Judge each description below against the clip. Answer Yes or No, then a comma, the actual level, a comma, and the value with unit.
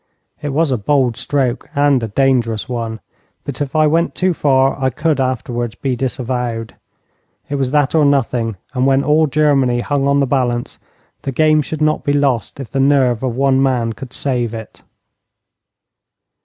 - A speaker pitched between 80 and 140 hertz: Yes, low, 135 Hz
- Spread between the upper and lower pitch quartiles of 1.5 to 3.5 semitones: Yes, average, 2.9 semitones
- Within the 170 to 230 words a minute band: Yes, average, 175 wpm